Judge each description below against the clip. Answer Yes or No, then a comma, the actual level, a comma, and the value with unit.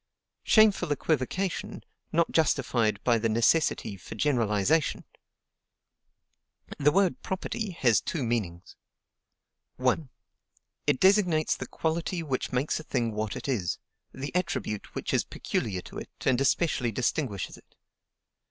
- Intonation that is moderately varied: No, wide, 6.4 semitones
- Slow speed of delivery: Yes, slow, 125 wpm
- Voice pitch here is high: No, low, 135 Hz